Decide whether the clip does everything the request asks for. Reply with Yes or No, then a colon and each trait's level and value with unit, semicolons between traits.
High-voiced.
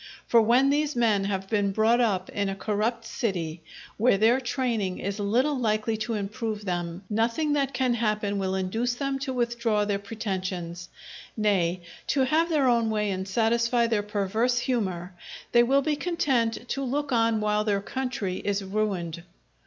Yes: high, 220 Hz